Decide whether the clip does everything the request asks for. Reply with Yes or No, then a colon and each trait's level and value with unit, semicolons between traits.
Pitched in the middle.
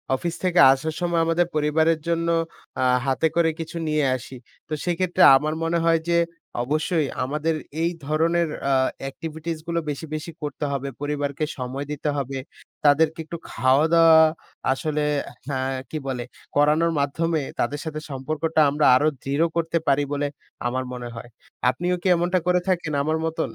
Yes: medium, 155 Hz